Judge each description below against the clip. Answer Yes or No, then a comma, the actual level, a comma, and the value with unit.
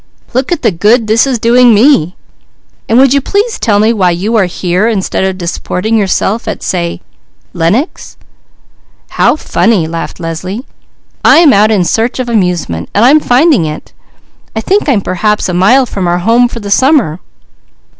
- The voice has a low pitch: No, high, 215 Hz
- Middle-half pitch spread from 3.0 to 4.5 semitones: No, average, 5.3 semitones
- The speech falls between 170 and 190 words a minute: Yes, average, 175 wpm